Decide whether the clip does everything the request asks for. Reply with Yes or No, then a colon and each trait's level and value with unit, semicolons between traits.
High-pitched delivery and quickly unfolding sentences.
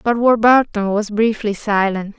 No: high, 215 Hz; slow, 135 wpm